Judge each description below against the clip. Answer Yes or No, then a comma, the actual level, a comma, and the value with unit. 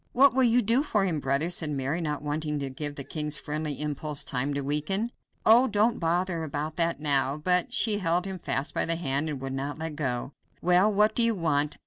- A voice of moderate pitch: Yes, medium, 155 Hz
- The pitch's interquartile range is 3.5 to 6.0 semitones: Yes, average, 4.5 semitones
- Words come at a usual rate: No, fast, 225 wpm